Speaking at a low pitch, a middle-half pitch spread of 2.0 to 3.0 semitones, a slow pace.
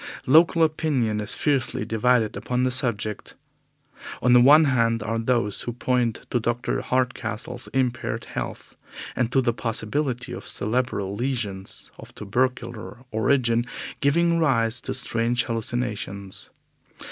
Yes: low, 120 Hz; narrow, 2.4 semitones; slow, 125 wpm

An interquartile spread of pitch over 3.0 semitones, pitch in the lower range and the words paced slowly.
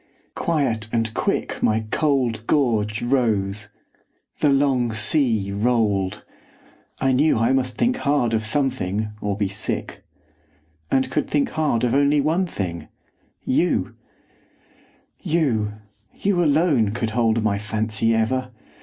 Yes: average, 4.6 semitones; low, 120 Hz; slow, 125 wpm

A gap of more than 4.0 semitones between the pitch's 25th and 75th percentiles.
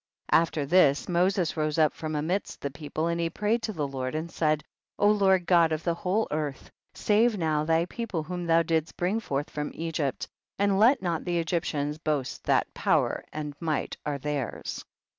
No: average, 3.3 semitones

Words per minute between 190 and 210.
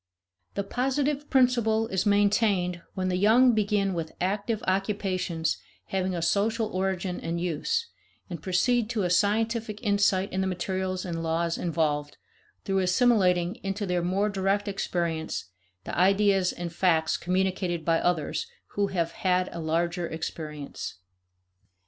No: slow, 135 wpm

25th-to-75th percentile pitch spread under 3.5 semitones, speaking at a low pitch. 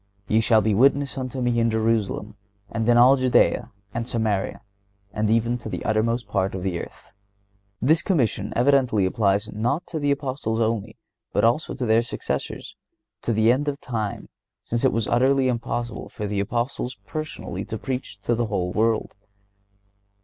Yes: average, 3.1 semitones; low, 115 Hz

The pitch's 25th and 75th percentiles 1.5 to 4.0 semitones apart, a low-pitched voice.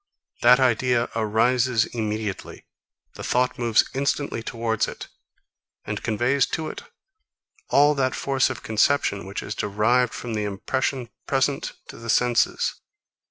Yes: average, 2.8 semitones; low, 120 Hz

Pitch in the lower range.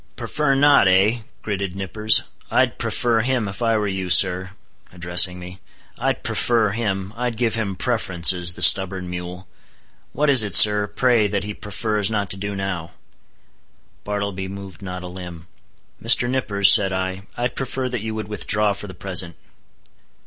Yes: low, 100 Hz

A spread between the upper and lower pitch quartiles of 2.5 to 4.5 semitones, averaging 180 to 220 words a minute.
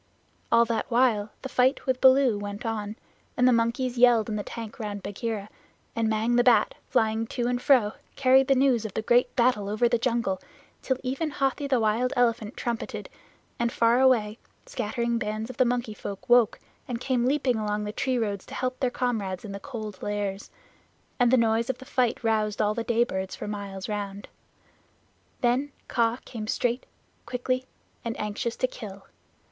Yes: average, 2.9 semitones; average, 185 wpm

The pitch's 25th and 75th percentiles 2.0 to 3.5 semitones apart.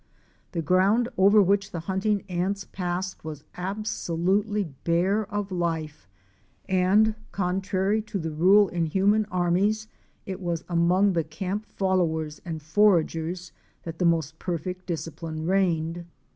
Yes: average, 3.0 semitones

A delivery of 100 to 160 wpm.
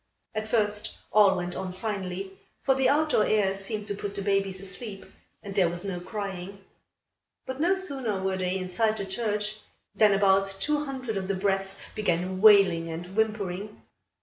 No: average, 170 wpm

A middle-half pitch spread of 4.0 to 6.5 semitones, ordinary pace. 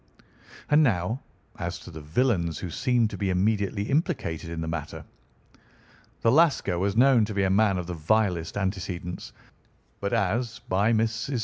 Yes: average, 4.6 semitones; average, 170 wpm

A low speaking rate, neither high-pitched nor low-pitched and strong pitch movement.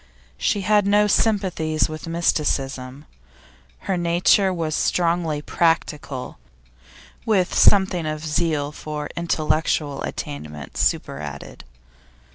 No: slow, 90 wpm; medium, 160 Hz; average, 3.5 semitones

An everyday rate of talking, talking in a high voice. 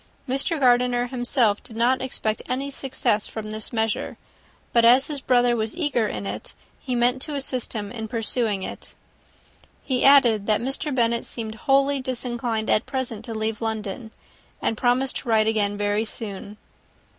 Yes: average, 165 wpm; high, 235 Hz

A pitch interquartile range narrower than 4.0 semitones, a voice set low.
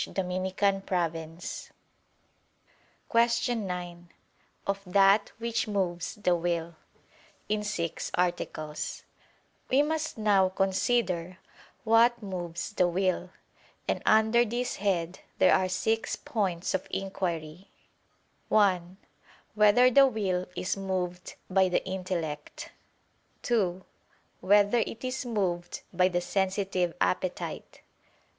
No: average, 3.1 semitones; high, 190 Hz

